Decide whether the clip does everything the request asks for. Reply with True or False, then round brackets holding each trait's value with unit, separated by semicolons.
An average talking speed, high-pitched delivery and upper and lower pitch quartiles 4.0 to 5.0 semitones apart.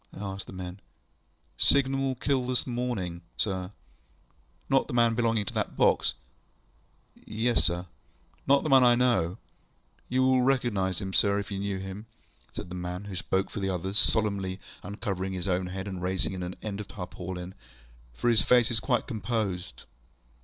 False (175 wpm; 100 Hz; 4.5 semitones)